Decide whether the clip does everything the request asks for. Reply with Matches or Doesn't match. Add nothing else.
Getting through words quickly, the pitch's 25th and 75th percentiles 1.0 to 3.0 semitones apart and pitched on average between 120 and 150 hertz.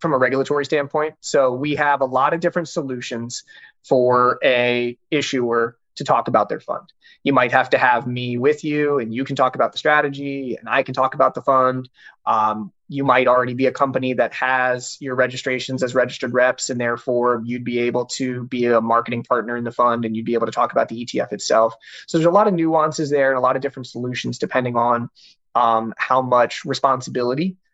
Matches